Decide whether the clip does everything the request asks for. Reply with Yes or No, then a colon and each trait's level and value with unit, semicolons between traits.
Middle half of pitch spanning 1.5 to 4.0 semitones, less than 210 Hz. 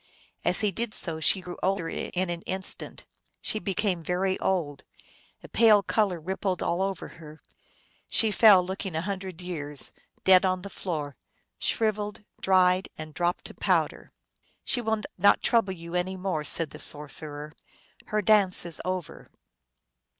Yes: average, 2.8 semitones; medium, 185 Hz